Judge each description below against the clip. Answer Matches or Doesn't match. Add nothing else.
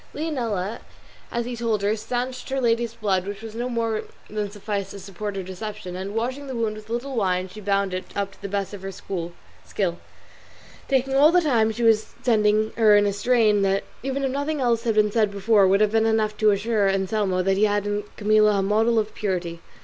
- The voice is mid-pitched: Doesn't match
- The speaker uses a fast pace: Matches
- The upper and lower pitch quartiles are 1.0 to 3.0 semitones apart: Matches